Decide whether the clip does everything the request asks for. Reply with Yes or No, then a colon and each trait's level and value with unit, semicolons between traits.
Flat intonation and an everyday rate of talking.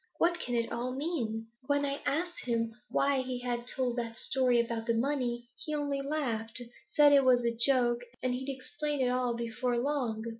No: average, 3.0 semitones; average, 190 wpm